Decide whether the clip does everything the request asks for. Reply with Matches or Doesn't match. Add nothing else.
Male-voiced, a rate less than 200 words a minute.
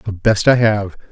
Doesn't match